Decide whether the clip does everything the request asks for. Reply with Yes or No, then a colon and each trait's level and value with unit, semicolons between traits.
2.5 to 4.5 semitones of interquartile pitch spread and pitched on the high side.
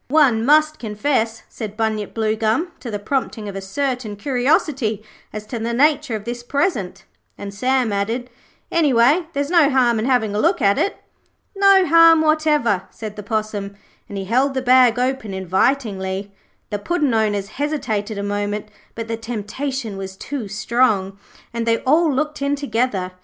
No: average, 5.2 semitones; high, 235 Hz